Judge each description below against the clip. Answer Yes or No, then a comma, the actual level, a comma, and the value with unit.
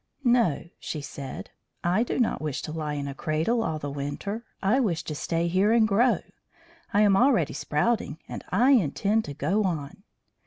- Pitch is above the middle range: No, medium, 180 Hz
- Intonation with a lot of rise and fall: Yes, wide, 6.7 semitones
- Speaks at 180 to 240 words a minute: Yes, average, 185 wpm